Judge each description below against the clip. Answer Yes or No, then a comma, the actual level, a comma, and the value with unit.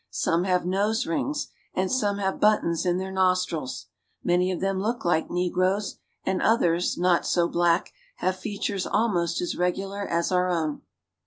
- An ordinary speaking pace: Yes, average, 160 wpm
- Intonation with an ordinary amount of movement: No, narrow, 2.3 semitones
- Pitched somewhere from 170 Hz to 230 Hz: Yes, medium, 185 Hz